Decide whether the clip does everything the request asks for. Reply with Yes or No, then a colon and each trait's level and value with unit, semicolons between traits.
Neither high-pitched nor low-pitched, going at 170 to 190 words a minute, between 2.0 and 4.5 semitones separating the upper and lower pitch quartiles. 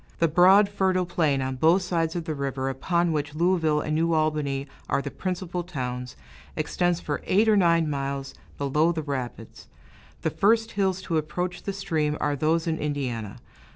Yes: medium, 160 Hz; average, 175 wpm; average, 3.9 semitones